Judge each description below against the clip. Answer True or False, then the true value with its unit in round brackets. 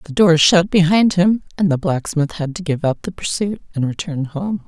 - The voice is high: False (180 Hz)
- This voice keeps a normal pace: False (220 wpm)